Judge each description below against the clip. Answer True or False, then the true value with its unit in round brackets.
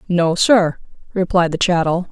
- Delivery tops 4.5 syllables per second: False (4.4 syllables/s)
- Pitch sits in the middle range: True (175 Hz)